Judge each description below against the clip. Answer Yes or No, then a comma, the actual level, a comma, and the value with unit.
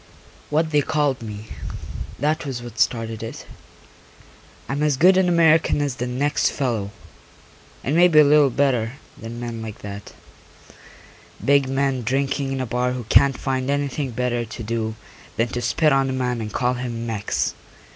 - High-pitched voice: No, low, 130 Hz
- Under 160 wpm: No, average, 170 wpm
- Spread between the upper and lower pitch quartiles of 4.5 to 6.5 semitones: No, average, 3.6 semitones